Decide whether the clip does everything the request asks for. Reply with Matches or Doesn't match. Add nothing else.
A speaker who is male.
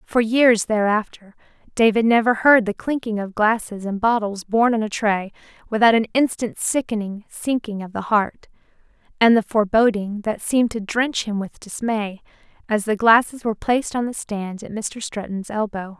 Doesn't match